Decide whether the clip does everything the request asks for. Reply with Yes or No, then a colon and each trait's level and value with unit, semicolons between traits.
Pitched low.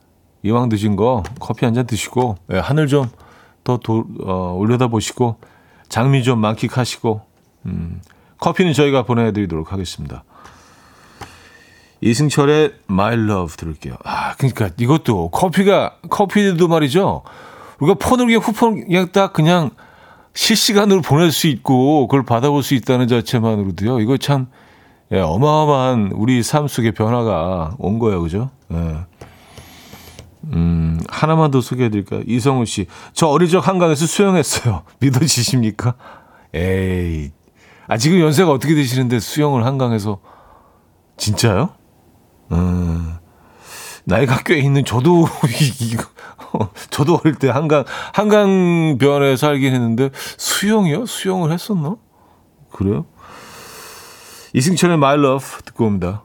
Yes: low, 125 Hz